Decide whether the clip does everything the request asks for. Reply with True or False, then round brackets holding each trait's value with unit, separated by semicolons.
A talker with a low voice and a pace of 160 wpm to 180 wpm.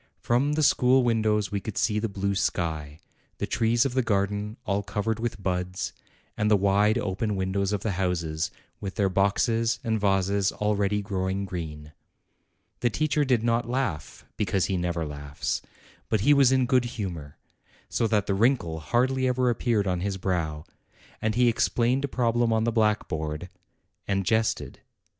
True (105 Hz; 165 wpm)